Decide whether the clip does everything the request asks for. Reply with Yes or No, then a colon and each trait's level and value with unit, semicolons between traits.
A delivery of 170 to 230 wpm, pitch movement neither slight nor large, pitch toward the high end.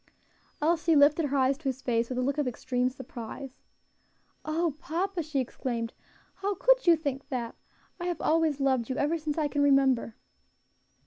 Yes: average, 175 wpm; average, 3.8 semitones; very high, 285 Hz